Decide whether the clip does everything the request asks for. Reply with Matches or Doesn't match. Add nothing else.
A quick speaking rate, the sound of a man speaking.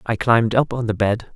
Matches